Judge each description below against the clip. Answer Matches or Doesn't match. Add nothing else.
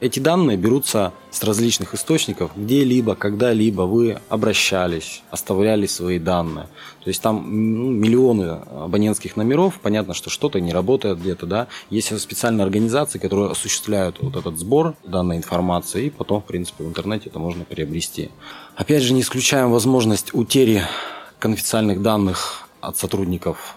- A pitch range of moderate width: Matches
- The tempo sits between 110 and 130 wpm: Doesn't match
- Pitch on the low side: Matches